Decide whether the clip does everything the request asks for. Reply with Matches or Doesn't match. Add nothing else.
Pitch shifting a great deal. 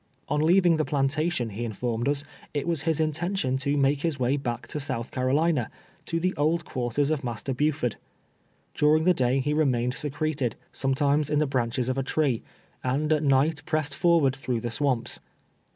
Doesn't match